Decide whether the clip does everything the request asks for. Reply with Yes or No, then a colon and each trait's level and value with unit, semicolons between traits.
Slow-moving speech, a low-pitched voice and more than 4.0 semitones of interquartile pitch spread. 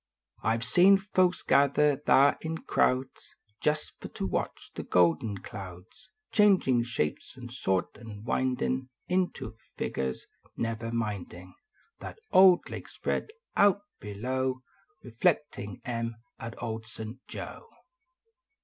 Yes: slow, 120 wpm; low, 120 Hz; average, 5.2 semitones